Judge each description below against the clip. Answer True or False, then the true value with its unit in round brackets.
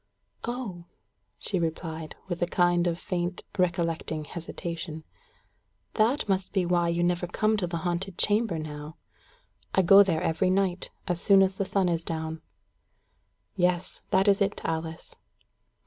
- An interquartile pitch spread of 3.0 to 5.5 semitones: False (2.6 semitones)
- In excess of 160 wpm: False (145 wpm)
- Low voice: False (175 Hz)